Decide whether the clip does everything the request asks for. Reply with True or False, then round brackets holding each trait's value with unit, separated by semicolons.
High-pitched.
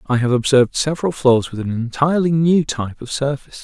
False (135 Hz)